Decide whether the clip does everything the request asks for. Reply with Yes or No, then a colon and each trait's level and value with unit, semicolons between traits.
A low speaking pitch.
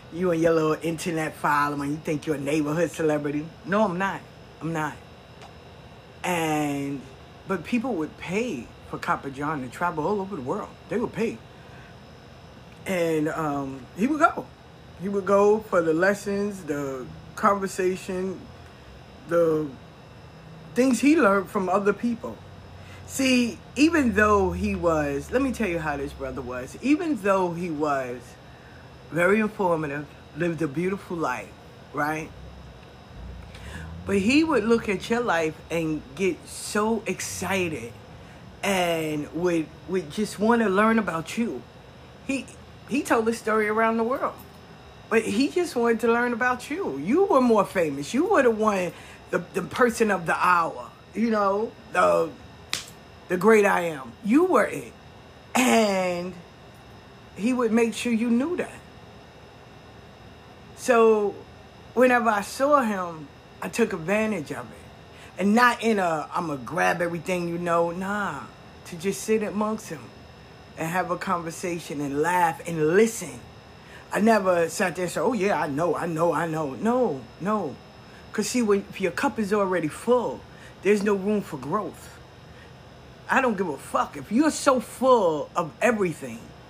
No: medium, 185 Hz